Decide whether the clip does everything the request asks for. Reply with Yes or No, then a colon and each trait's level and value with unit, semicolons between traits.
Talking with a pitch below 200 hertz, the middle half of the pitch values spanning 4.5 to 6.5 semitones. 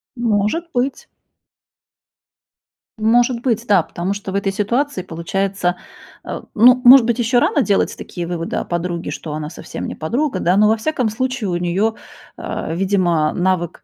No: high, 205 Hz; wide, 5.4 semitones